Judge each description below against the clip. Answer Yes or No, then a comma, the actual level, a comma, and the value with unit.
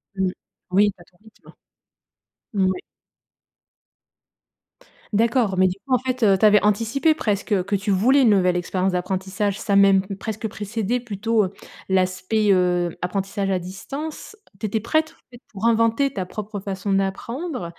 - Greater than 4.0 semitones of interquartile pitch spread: No, average, 3.2 semitones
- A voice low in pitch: No, high, 200 Hz